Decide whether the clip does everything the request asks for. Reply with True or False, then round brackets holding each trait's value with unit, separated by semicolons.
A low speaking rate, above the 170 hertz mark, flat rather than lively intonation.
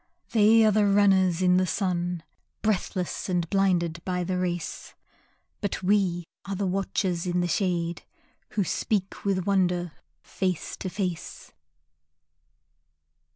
True (120 wpm; 185 Hz; 2.0 semitones)